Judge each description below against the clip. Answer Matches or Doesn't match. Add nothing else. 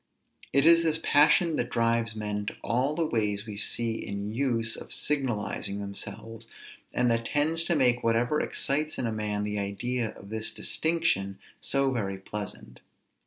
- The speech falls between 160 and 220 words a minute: Matches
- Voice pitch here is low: Matches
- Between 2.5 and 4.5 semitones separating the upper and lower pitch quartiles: Doesn't match